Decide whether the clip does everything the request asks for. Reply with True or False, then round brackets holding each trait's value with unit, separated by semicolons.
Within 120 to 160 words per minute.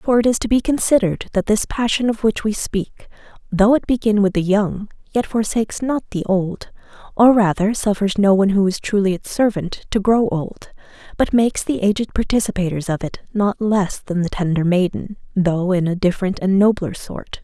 False (195 wpm)